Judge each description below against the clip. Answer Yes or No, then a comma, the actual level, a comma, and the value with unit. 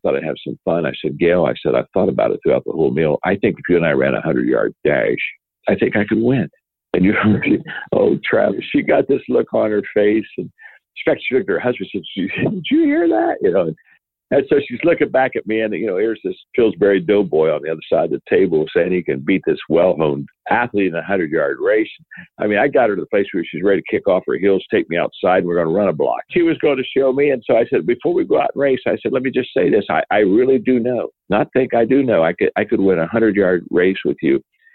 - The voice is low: Yes, low, 125 Hz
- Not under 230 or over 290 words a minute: Yes, fast, 275 wpm